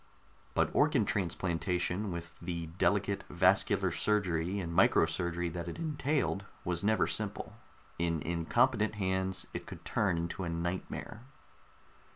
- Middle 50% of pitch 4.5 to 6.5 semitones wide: No, average, 3.1 semitones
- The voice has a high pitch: No, very low, 90 Hz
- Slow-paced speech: Yes, slow, 130 wpm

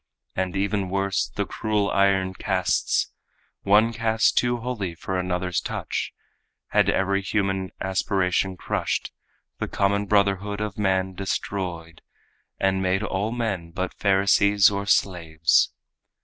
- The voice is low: Yes, very low, 95 Hz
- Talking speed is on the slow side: Yes, slow, 120 wpm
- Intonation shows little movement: Yes, narrow, 1.6 semitones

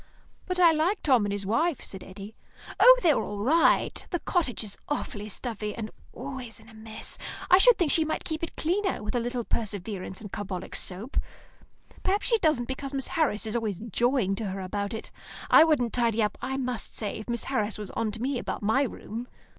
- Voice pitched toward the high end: Yes, high, 235 Hz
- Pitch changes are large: Yes, wide, 5.8 semitones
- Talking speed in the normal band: No, fast, 210 wpm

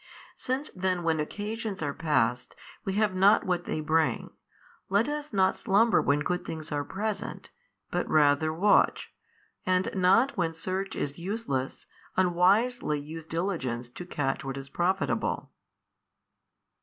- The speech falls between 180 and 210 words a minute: No, slow, 135 wpm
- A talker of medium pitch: Yes, medium, 180 Hz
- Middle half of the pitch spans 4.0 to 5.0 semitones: Yes, average, 4.7 semitones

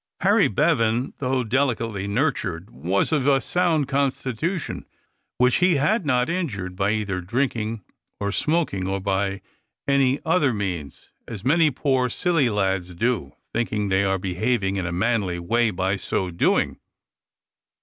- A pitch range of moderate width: No, wide, 5.9 semitones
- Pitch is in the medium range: No, low, 115 Hz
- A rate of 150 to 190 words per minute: No, average, 140 wpm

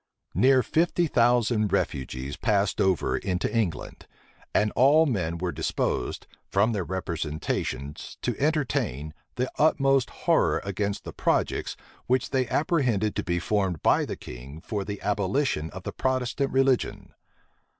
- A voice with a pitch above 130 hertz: No, low, 105 Hz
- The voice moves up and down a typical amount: No, wide, 6.9 semitones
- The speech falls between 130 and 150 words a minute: Yes, slow, 135 wpm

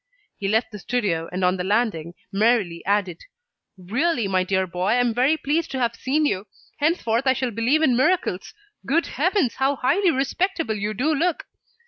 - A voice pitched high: Yes, high, 240 Hz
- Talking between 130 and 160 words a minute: No, average, 180 wpm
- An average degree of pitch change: No, wide, 6.8 semitones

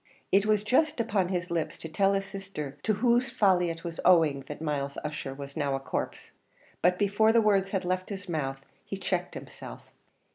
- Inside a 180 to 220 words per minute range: Yes, average, 195 wpm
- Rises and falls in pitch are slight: No, average, 4.8 semitones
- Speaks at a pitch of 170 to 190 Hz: Yes, medium, 185 Hz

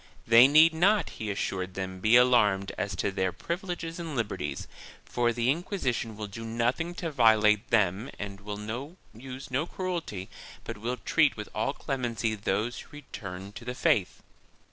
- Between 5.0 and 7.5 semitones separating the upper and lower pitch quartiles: Yes, wide, 5.5 semitones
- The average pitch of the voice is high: No, low, 115 Hz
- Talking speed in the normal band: Yes, average, 165 wpm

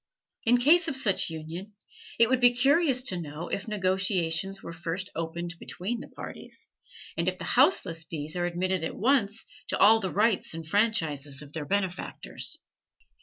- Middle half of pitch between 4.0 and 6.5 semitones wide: Yes, wide, 5.5 semitones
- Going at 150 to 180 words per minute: Yes, average, 170 wpm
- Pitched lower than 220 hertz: Yes, high, 190 Hz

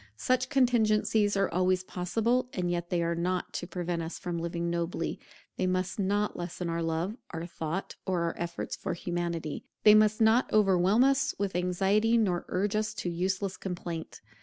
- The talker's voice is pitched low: No, medium, 185 Hz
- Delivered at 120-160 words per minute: No, average, 175 wpm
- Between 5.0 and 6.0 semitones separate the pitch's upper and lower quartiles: No, average, 3.5 semitones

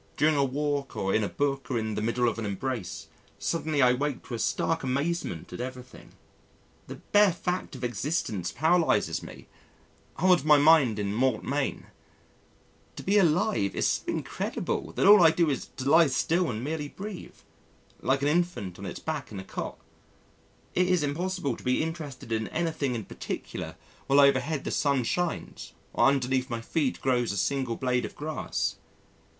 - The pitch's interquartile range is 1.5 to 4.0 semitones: No, average, 4.7 semitones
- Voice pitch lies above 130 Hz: Yes, medium, 140 Hz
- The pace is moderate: Yes, average, 180 wpm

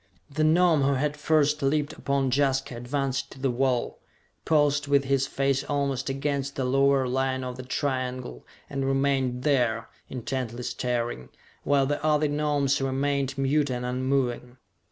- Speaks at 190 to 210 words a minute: No, average, 150 wpm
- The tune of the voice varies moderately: No, narrow, 1.8 semitones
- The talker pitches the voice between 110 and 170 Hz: Yes, low, 135 Hz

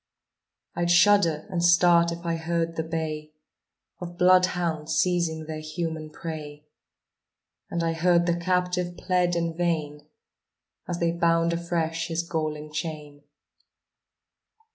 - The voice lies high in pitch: No, medium, 170 Hz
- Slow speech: Yes, slow, 120 wpm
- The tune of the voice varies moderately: No, narrow, 1.6 semitones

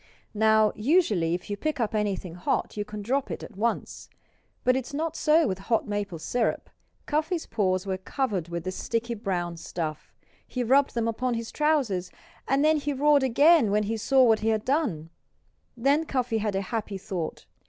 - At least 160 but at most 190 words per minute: Yes, average, 185 wpm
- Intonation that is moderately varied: No, wide, 5.7 semitones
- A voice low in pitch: No, high, 225 Hz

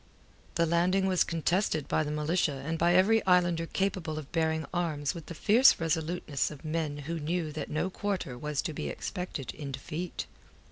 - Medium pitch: Yes, medium, 165 Hz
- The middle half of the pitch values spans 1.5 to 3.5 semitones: Yes, average, 2.9 semitones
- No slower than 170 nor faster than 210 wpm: Yes, average, 180 wpm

